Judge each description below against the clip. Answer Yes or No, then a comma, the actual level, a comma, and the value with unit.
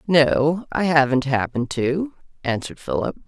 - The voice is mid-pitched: Yes, medium, 150 Hz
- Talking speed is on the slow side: Yes, slow, 130 wpm